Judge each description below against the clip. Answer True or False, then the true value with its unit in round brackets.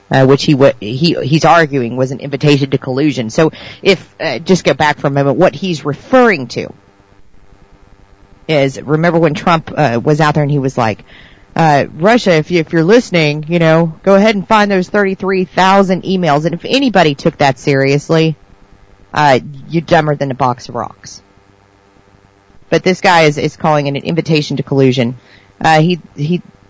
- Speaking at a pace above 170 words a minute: True (185 wpm)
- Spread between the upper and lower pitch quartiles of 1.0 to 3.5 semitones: False (4.9 semitones)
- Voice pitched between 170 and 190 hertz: False (150 Hz)